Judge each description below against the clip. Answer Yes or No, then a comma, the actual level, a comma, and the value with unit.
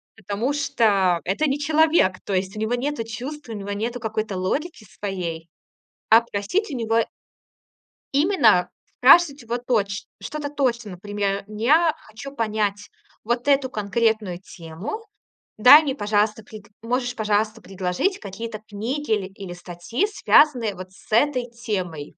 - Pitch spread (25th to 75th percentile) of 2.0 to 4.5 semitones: No, average, 5.1 semitones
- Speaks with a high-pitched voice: Yes, high, 220 Hz